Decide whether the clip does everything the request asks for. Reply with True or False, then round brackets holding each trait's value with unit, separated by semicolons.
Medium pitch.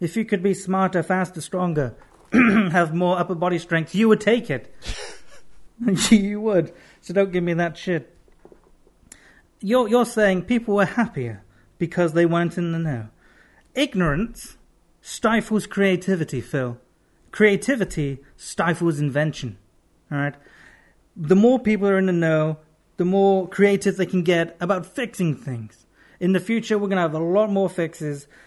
True (180 Hz)